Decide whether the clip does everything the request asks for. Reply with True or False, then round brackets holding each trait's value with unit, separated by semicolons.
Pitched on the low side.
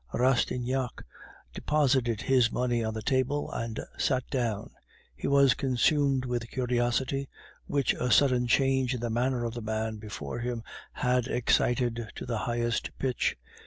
True (125 Hz)